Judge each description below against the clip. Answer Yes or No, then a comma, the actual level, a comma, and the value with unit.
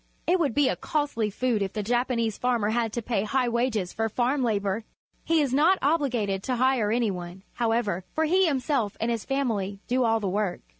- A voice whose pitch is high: Yes, high, 235 Hz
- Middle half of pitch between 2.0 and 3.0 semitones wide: No, average, 3.9 semitones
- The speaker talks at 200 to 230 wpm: Yes, fast, 205 wpm